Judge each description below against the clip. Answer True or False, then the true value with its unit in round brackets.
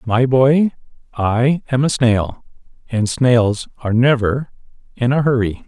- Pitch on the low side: True (125 Hz)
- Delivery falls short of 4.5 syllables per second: True (4.0 syllables/s)